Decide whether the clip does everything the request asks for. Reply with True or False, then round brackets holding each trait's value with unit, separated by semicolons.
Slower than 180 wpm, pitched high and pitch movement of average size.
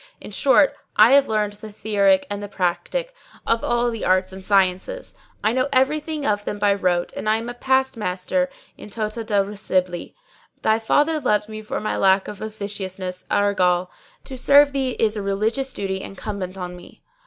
False (185 wpm; 210 Hz; 4.1 semitones)